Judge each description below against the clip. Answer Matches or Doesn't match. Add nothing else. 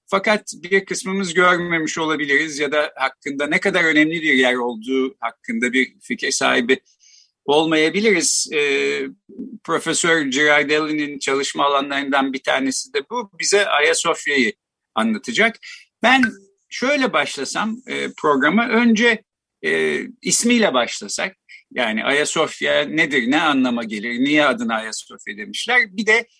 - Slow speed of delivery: Doesn't match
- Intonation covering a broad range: Matches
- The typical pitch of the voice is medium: Matches